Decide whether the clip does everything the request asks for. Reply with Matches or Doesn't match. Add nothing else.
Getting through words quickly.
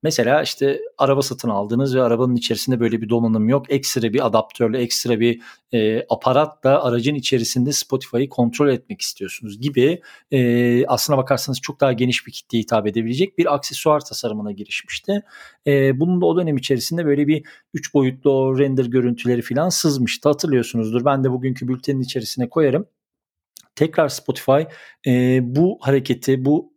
Matches